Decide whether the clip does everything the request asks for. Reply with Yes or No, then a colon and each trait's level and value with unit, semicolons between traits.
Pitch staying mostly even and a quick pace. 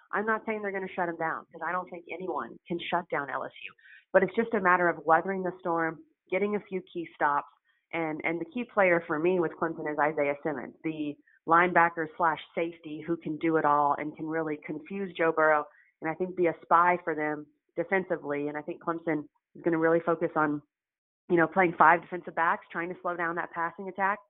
Yes: narrow, 2.3 semitones; fast, 220 wpm